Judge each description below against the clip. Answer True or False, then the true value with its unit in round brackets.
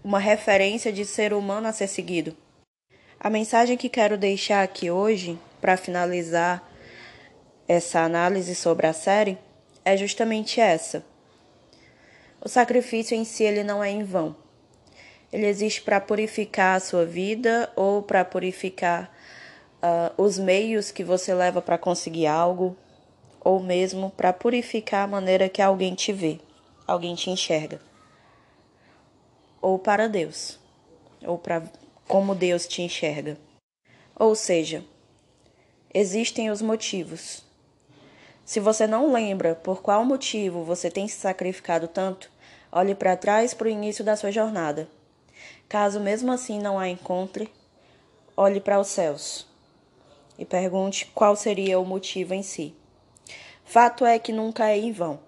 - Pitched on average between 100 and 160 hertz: False (195 Hz)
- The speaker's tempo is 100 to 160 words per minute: True (135 wpm)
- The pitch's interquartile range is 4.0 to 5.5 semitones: False (3.1 semitones)